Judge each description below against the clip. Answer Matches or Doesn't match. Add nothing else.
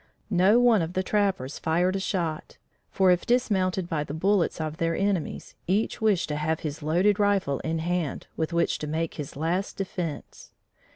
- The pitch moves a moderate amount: Matches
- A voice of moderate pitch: Matches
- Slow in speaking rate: Doesn't match